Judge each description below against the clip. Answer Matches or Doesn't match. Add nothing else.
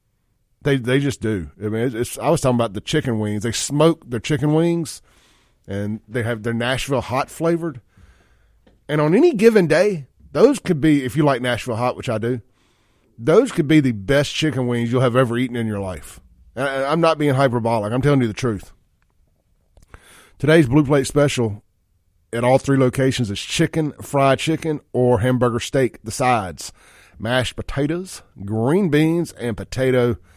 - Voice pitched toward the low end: Matches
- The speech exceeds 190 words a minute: Doesn't match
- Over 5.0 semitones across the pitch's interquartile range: Doesn't match